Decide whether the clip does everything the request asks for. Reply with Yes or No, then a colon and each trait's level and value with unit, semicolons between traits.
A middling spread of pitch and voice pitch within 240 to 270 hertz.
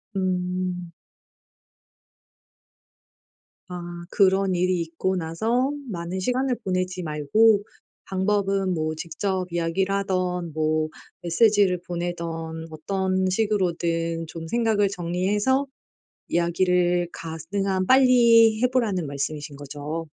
No: average, 3.0 semitones; medium, 185 Hz